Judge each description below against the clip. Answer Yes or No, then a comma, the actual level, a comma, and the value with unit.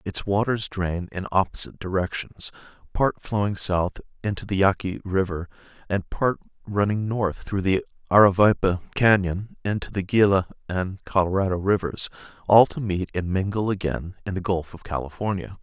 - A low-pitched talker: Yes, very low, 95 Hz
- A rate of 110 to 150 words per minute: Yes, average, 145 wpm